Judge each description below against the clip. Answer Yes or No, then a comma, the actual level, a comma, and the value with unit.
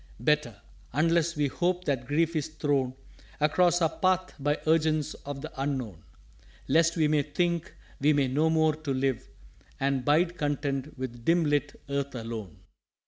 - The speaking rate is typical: Yes, average, 160 wpm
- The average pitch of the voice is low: No, medium, 150 Hz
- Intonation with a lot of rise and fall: No, average, 2.9 semitones